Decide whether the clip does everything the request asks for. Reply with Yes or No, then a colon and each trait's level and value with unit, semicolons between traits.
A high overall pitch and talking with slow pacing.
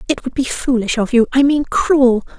No: very high, 255 Hz; average, 200 wpm